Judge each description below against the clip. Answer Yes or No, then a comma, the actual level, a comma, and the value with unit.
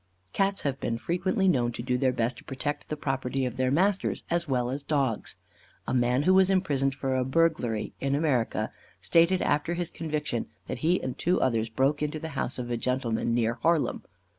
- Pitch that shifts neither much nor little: Yes, average, 4.8 semitones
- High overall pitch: No, low, 135 Hz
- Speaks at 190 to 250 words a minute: Yes, average, 200 wpm